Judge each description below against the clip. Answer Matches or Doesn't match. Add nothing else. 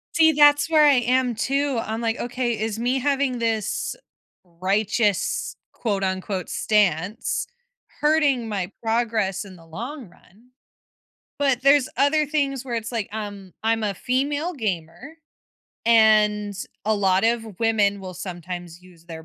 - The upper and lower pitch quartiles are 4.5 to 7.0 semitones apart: Matches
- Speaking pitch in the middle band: Doesn't match